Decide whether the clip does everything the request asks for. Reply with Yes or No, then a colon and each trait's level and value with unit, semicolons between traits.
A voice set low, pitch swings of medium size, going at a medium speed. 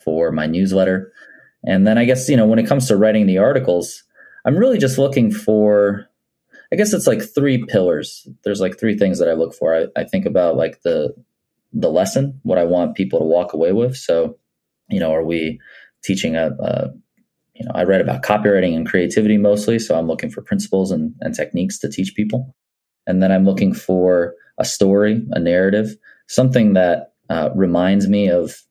Yes: low, 100 Hz; average, 3.1 semitones; average, 195 wpm